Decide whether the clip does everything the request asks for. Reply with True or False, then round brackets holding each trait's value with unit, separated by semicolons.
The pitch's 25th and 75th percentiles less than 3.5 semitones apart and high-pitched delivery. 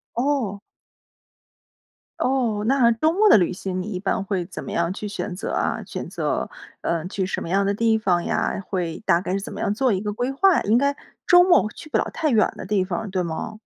False (5.1 semitones; 205 Hz)